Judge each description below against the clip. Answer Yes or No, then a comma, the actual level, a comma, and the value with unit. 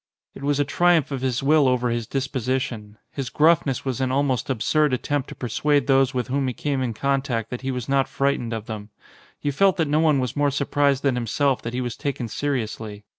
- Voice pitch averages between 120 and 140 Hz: Yes, low, 135 Hz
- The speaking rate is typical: No, fast, 225 wpm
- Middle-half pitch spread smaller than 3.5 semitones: Yes, average, 2.7 semitones